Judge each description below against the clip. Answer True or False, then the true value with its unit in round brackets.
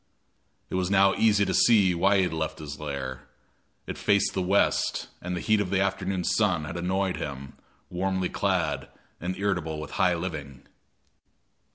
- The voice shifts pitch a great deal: False (3.7 semitones)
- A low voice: True (90 Hz)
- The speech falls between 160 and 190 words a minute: True (170 wpm)